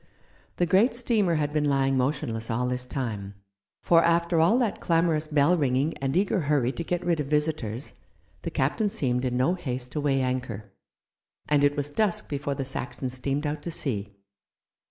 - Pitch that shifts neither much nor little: Yes, average, 4.6 semitones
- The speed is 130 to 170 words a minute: No, average, 180 wpm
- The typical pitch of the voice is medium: Yes, medium, 145 Hz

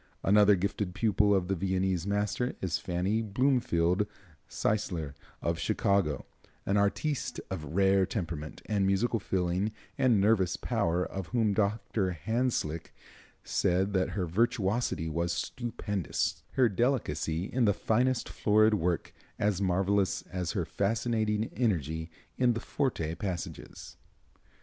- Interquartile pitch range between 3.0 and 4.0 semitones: Yes, average, 3.6 semitones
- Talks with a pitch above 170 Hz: No, low, 100 Hz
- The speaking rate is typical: No, slow, 120 wpm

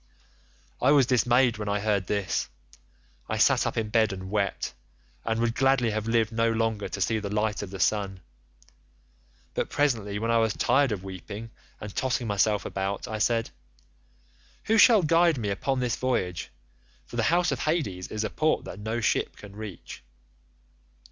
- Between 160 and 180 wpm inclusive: Yes, average, 175 wpm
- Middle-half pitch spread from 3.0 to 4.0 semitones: Yes, average, 3.3 semitones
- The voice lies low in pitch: Yes, low, 110 Hz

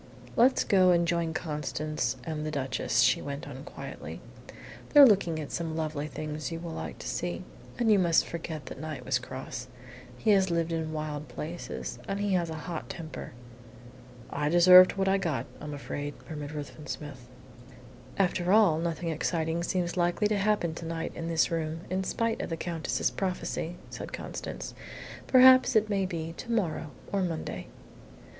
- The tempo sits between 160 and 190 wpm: Yes, average, 175 wpm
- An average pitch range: Yes, average, 3.2 semitones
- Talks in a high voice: No, medium, 165 Hz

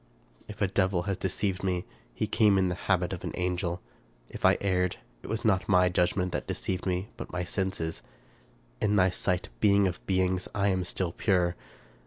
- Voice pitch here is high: No, very low, 95 Hz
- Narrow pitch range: Yes, narrow, 1.6 semitones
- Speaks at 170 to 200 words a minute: Yes, average, 185 wpm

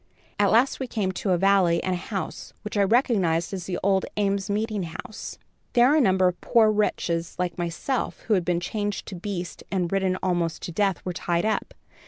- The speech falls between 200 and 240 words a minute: Yes, fast, 205 wpm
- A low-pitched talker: No, high, 190 Hz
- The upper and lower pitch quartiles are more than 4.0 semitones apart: No, average, 3.0 semitones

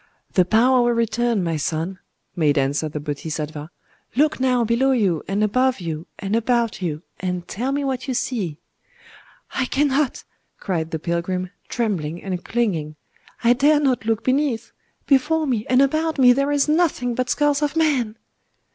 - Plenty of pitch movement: Yes, wide, 7.1 semitones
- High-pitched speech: Yes, high, 230 Hz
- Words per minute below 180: Yes, average, 165 wpm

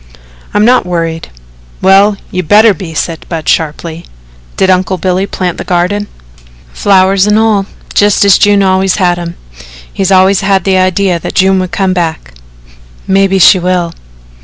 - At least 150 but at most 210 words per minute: Yes, average, 160 wpm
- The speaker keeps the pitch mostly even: Yes, narrow, 2.0 semitones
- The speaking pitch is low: No, high, 190 Hz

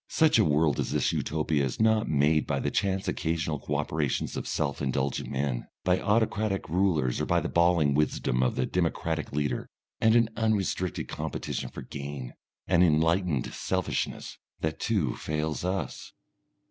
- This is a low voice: Yes, very low, 80 Hz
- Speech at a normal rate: Yes, average, 160 wpm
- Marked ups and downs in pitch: No, average, 4.5 semitones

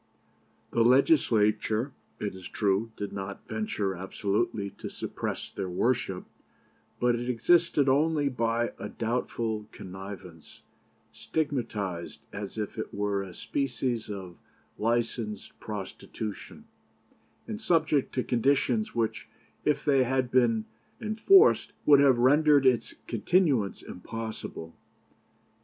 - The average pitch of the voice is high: No, low, 115 Hz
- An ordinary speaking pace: No, slow, 110 wpm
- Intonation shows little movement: No, average, 4.8 semitones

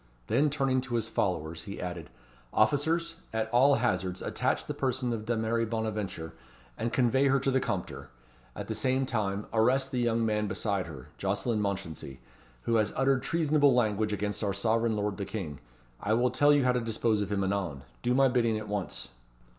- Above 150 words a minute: Yes, average, 185 wpm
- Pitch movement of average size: Yes, average, 4.3 semitones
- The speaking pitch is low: Yes, low, 110 Hz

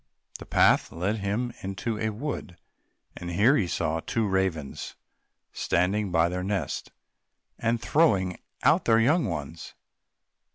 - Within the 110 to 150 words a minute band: Yes, slow, 135 wpm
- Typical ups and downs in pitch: Yes, average, 4.3 semitones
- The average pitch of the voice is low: Yes, low, 100 Hz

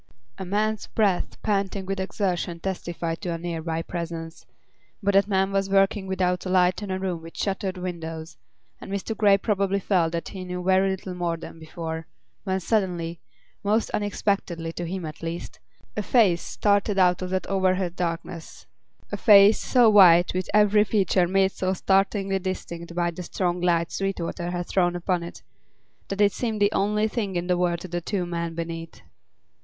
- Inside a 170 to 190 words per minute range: Yes, average, 180 wpm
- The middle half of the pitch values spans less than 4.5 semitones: Yes, narrow, 2.4 semitones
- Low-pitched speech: No, medium, 185 Hz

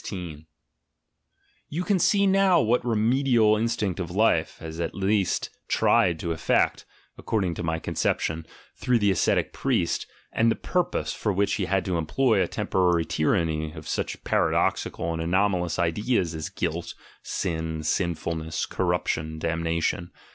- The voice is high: No, very low, 90 Hz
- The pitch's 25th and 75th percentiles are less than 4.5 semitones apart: No, average, 5.1 semitones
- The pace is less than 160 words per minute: Yes, average, 140 wpm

